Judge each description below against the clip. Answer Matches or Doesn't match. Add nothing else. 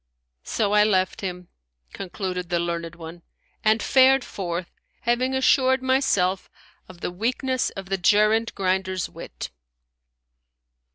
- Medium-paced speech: Doesn't match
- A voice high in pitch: Matches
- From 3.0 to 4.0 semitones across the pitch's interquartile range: Doesn't match